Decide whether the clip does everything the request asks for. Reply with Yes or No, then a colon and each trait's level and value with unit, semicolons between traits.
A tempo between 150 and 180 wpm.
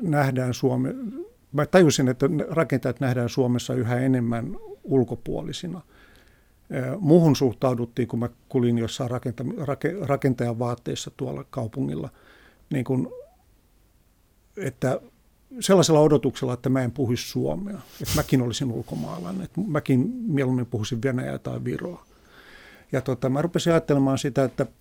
No: average, 120 wpm